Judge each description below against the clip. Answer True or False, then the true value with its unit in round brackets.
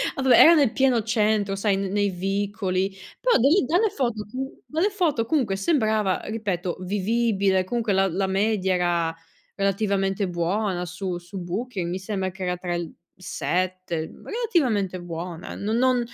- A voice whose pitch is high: True (200 Hz)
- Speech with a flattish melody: False (4.1 semitones)